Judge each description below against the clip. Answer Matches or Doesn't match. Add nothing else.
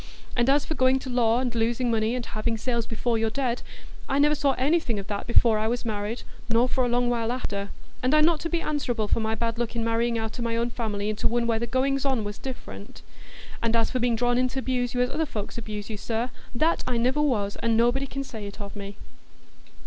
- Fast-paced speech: Matches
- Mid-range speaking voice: Doesn't match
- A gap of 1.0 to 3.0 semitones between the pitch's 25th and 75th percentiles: Matches